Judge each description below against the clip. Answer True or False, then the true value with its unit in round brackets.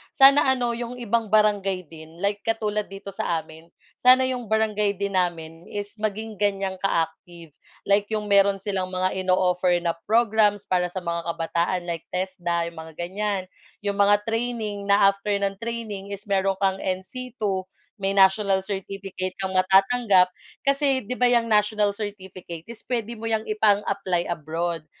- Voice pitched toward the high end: True (200 Hz)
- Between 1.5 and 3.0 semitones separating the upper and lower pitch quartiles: True (2.6 semitones)